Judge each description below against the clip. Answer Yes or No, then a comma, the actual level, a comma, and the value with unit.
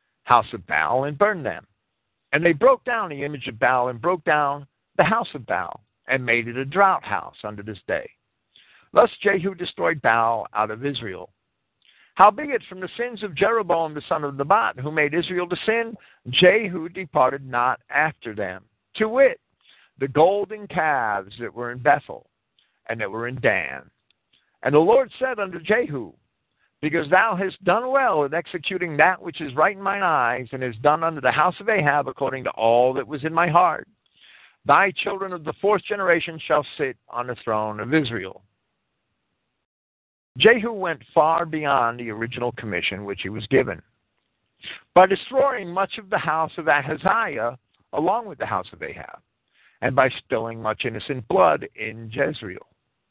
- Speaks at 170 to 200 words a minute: Yes, average, 175 wpm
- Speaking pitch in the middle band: Yes, medium, 150 Hz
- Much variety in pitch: Yes, wide, 7.6 semitones